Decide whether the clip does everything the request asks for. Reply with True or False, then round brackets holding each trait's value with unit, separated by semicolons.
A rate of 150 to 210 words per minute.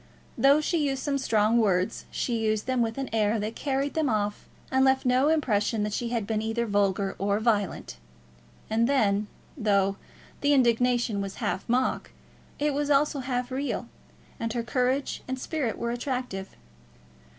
True (165 wpm)